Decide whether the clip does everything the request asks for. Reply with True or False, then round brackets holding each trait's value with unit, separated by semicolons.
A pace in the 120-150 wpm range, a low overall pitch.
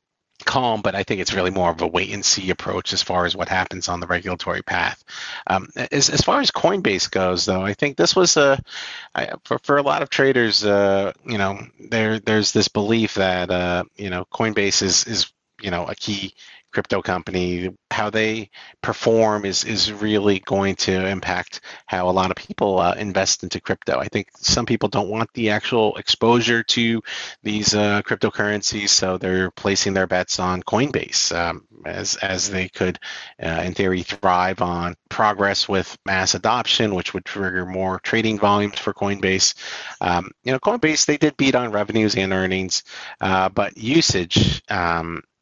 False (180 wpm; 100 Hz)